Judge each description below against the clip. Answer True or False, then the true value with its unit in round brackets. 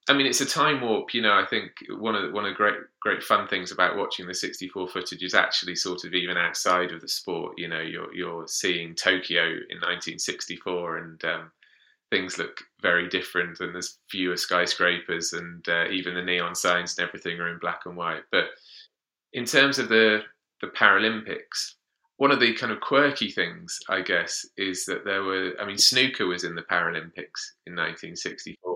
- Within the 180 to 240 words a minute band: True (195 wpm)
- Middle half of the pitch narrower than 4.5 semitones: True (3.6 semitones)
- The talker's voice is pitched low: True (90 Hz)